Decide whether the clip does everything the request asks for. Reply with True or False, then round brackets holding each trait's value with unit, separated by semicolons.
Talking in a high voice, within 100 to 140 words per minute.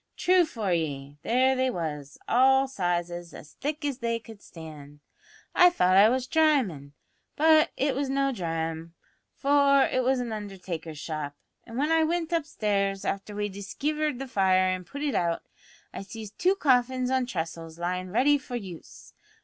False (220 Hz; 165 wpm)